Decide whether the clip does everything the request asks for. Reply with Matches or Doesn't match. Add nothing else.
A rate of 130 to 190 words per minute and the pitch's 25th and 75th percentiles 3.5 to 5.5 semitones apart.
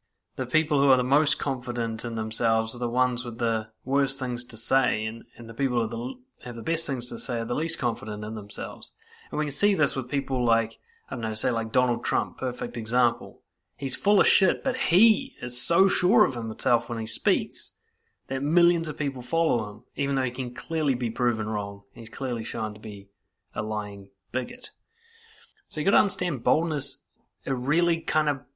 Doesn't match